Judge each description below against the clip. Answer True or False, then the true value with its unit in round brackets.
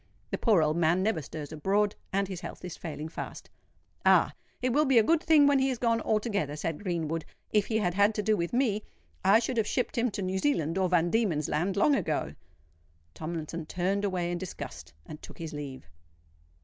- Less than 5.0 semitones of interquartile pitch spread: False (5.3 semitones)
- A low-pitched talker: False (190 Hz)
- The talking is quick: True (210 wpm)